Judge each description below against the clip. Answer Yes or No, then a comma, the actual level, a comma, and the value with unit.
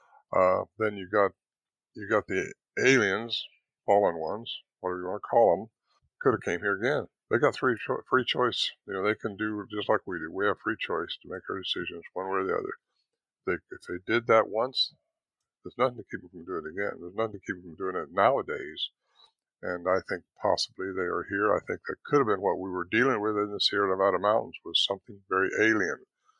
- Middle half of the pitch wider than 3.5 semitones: No, narrow, 2.6 semitones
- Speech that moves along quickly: Yes, fast, 225 wpm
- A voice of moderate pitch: No, low, 100 Hz